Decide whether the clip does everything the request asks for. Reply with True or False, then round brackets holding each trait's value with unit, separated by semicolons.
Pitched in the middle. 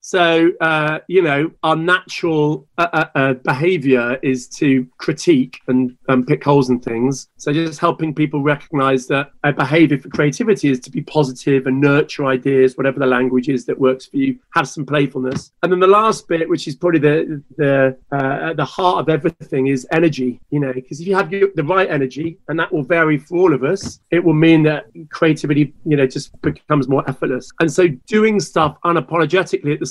True (150 Hz)